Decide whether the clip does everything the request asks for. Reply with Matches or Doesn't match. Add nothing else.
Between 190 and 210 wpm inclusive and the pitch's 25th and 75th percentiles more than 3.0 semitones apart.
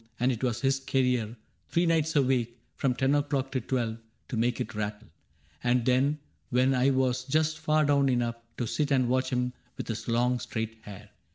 Doesn't match